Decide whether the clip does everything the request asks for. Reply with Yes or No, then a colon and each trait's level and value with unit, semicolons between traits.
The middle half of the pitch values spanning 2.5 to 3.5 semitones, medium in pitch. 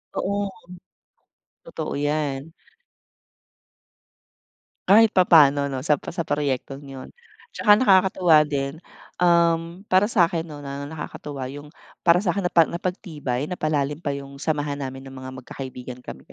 No: average, 4.0 semitones; medium, 150 Hz